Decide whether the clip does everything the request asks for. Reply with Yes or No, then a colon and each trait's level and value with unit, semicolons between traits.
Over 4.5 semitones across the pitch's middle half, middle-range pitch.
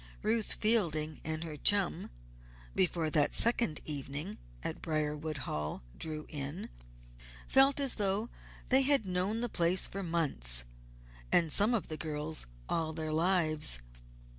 Yes: average, 4.9 semitones; medium, 160 Hz